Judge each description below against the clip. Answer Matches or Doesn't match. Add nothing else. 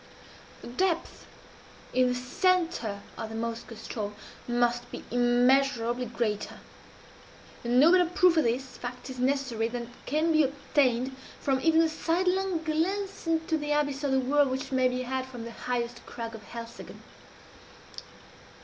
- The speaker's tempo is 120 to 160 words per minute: Matches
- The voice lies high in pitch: Matches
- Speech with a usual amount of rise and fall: Matches